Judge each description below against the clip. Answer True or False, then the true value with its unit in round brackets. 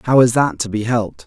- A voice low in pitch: True (115 Hz)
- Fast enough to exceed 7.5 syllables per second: False (6.2 syllables/s)